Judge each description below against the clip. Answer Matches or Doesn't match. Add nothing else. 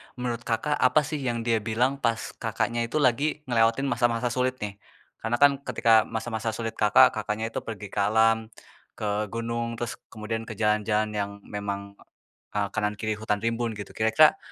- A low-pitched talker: Matches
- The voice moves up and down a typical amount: Doesn't match